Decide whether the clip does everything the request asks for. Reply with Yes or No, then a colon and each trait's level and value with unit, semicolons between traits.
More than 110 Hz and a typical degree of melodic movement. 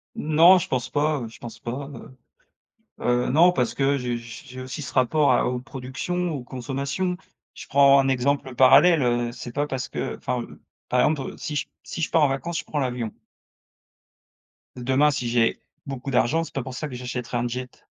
Yes: low, 130 Hz; average, 3.0 semitones